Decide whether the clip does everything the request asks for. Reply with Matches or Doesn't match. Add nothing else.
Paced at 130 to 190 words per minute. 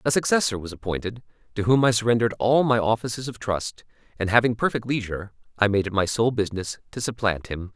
Doesn't match